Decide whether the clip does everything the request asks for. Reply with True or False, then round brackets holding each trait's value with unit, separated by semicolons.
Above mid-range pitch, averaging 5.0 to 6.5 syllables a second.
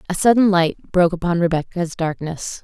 False (175 Hz; 5.4 syllables/s)